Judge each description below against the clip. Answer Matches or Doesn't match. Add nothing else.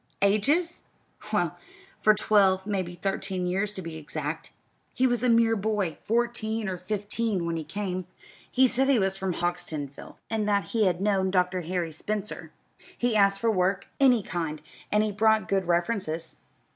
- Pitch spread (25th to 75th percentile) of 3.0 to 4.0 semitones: Matches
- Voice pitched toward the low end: Doesn't match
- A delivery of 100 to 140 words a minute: Doesn't match